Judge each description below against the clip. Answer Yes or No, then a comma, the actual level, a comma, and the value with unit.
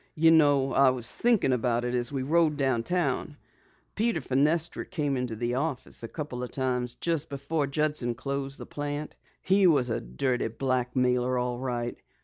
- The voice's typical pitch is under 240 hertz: Yes, low, 135 Hz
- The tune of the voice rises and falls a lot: No, average, 3.4 semitones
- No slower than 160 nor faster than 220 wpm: Yes, average, 165 wpm